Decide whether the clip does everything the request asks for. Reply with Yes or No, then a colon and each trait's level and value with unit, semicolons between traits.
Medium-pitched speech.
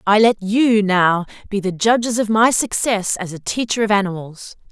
No: high, 205 Hz